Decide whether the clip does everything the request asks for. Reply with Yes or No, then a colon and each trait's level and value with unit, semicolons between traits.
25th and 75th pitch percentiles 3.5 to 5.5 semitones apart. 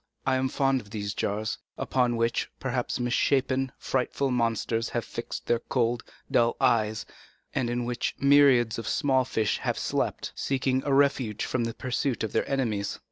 No: narrow, 2.4 semitones